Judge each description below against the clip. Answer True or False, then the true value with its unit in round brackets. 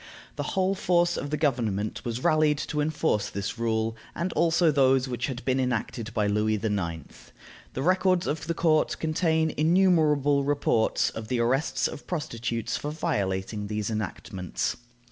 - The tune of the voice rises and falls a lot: True (6.2 semitones)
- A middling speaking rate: True (155 wpm)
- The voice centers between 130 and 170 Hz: True (135 Hz)